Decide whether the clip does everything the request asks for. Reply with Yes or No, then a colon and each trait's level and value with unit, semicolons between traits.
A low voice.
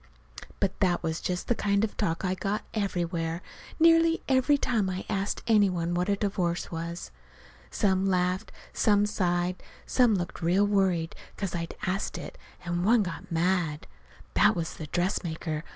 No: medium, 185 Hz